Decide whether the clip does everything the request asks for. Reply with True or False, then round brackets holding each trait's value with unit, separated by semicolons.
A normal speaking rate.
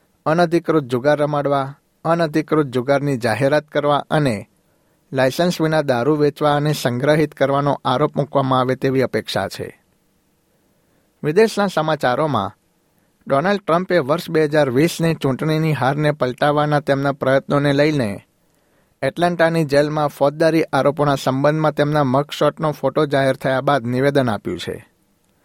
True (115 wpm)